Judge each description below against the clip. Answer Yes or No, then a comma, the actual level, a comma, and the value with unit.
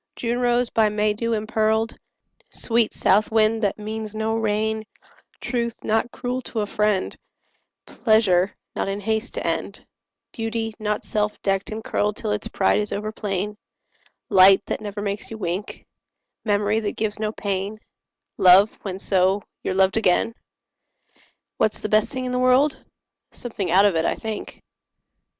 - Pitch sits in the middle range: No, high, 215 Hz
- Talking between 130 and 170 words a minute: Yes, average, 160 wpm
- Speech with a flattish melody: Yes, narrow, 1.8 semitones